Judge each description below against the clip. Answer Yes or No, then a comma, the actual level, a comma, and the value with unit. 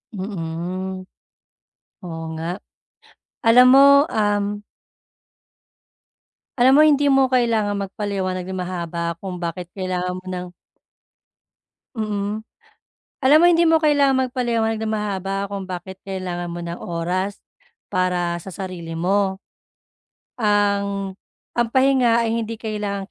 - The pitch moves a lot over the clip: No, average, 3.8 semitones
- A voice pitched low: No, high, 200 Hz